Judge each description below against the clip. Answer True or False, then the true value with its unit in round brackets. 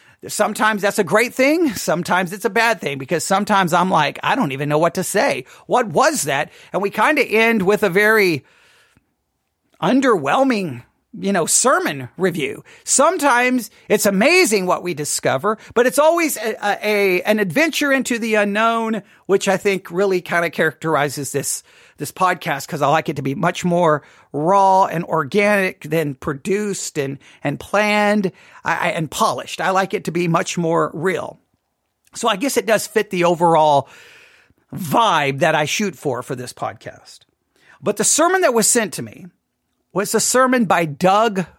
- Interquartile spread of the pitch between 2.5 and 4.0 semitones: False (4.7 semitones)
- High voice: True (195 Hz)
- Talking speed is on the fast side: False (175 wpm)